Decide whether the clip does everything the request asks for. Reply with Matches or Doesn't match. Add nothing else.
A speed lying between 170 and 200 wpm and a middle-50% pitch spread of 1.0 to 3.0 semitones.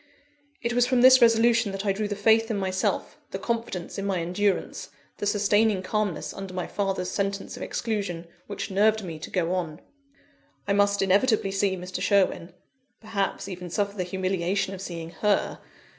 Matches